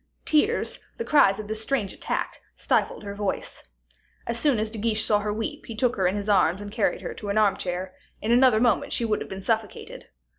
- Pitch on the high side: Yes, high, 215 Hz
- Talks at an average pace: No, fast, 220 wpm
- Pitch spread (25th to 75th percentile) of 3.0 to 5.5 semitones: No, narrow, 2.5 semitones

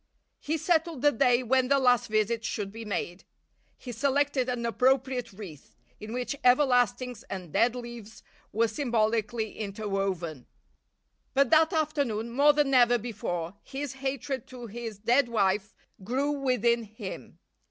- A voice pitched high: Yes, high, 240 Hz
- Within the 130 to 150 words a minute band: Yes, average, 140 wpm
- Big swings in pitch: No, average, 3.8 semitones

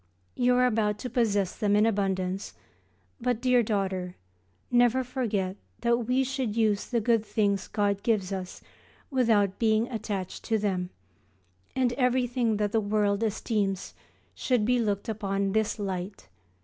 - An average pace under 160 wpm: Yes, average, 150 wpm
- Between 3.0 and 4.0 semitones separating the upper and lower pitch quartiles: Yes, average, 3.3 semitones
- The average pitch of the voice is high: Yes, high, 215 Hz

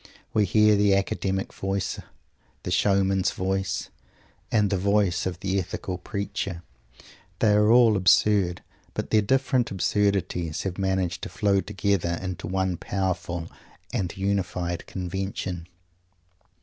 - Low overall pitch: Yes, very low, 95 Hz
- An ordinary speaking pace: No, slow, 125 wpm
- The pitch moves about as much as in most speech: No, narrow, 1.9 semitones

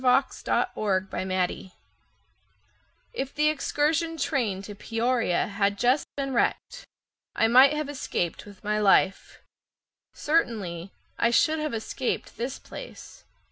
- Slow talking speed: Yes, slow, 115 wpm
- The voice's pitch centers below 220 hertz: No, high, 235 Hz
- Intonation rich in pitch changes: Yes, wide, 6.3 semitones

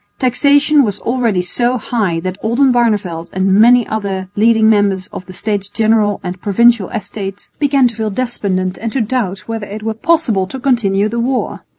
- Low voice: No, high, 220 Hz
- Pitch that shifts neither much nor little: Yes, average, 3.8 semitones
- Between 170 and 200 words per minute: Yes, average, 175 wpm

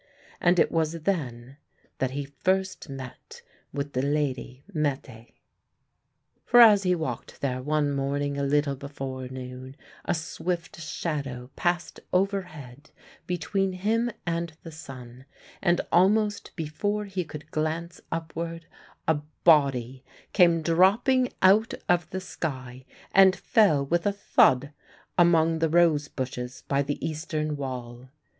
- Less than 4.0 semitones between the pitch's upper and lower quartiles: No, average, 4.5 semitones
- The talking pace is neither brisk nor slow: No, slow, 130 wpm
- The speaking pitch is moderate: Yes, medium, 155 Hz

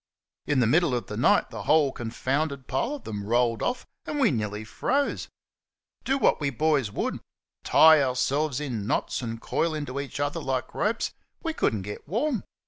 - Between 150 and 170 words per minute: No, average, 185 wpm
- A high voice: No, medium, 140 Hz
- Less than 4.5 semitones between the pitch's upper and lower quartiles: No, average, 5.0 semitones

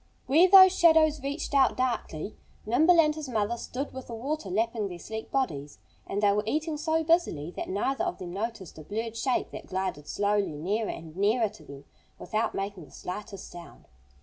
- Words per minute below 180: No, average, 190 wpm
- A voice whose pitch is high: Yes, high, 225 Hz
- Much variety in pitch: Yes, wide, 7.1 semitones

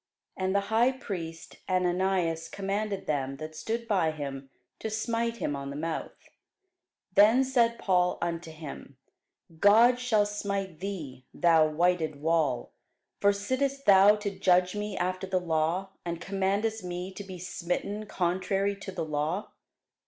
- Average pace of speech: Yes, average, 145 wpm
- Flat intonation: No, average, 4.0 semitones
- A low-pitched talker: No, medium, 185 Hz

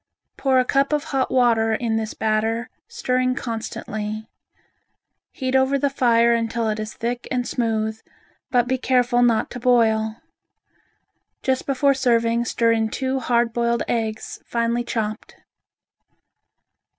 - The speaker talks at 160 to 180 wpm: No, slow, 135 wpm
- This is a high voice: Yes, high, 235 Hz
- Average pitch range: No, narrow, 2.3 semitones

